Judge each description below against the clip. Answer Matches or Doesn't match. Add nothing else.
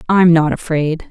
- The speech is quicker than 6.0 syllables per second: Doesn't match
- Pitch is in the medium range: Matches